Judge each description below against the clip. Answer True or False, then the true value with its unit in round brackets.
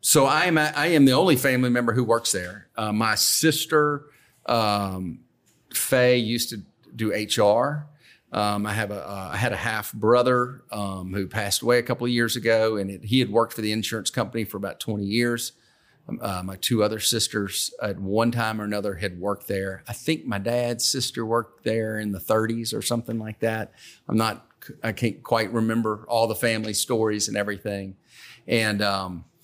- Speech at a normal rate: True (195 wpm)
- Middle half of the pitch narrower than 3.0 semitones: True (2.6 semitones)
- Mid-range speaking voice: False (110 Hz)